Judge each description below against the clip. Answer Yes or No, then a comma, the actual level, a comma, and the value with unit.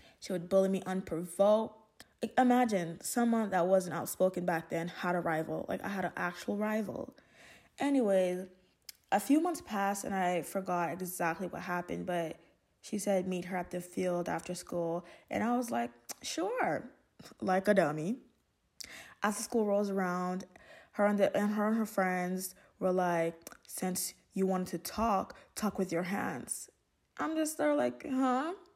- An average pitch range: Yes, average, 3.5 semitones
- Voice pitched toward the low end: No, high, 190 Hz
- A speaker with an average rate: Yes, average, 165 wpm